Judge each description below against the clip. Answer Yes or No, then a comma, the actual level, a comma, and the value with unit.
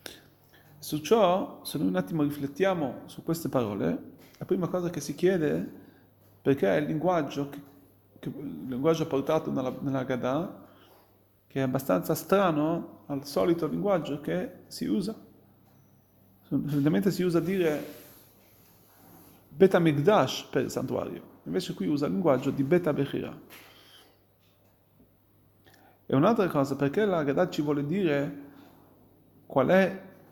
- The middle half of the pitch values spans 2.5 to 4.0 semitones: No, average, 4.6 semitones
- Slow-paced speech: No, average, 135 wpm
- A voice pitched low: No, medium, 145 Hz